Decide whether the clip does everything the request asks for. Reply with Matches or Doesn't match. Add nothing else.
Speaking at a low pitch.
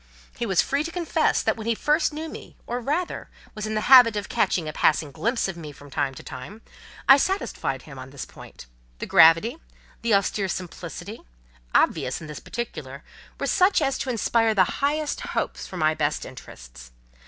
Doesn't match